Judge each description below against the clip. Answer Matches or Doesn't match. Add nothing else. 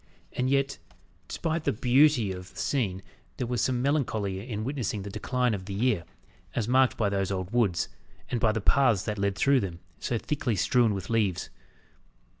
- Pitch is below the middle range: Matches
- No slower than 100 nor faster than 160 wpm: Doesn't match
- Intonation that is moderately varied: Matches